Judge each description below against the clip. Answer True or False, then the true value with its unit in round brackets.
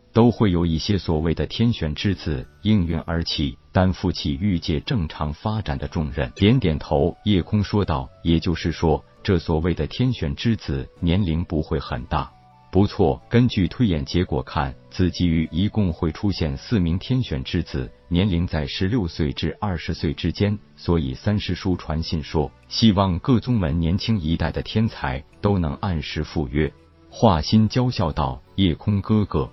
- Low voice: True (85 Hz)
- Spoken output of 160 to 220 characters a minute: False (250 characters per minute)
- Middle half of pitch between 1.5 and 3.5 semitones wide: False (4.8 semitones)